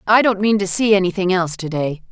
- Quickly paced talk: Yes, fast, 255 wpm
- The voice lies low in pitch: No, high, 190 Hz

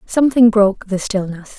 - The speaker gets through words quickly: No, average, 150 wpm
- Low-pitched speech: No, high, 210 Hz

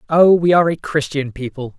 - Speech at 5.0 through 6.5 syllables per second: Yes, 5.7 syllables/s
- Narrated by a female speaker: No, male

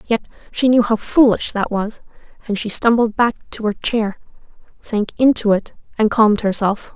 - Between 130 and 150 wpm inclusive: No, average, 175 wpm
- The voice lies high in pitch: Yes, high, 220 Hz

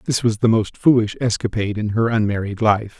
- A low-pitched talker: Yes, low, 110 Hz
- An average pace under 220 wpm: Yes, average, 200 wpm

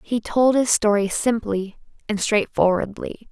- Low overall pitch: No, high, 215 Hz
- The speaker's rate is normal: No, slow, 125 wpm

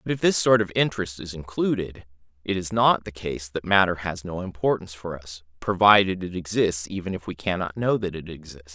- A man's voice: Yes, male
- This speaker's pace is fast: Yes, fast, 215 wpm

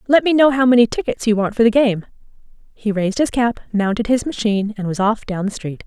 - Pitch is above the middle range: Yes, high, 225 Hz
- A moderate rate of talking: No, fast, 245 wpm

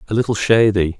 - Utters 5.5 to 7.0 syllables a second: Yes, 6.2 syllables/s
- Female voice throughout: No, male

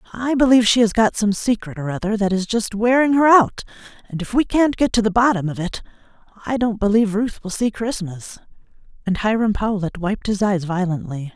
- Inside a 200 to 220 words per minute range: Yes, fast, 205 wpm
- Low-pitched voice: No, high, 210 Hz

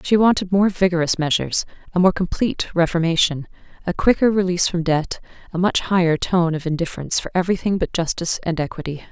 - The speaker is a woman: Yes, female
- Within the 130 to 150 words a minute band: No, average, 170 wpm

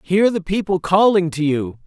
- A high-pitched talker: No, medium, 175 Hz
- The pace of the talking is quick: No, average, 195 wpm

